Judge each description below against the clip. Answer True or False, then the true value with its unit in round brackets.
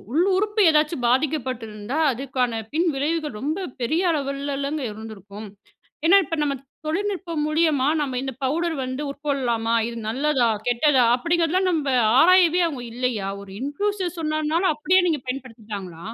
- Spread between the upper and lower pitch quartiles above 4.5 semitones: True (4.9 semitones)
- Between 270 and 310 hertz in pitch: True (285 Hz)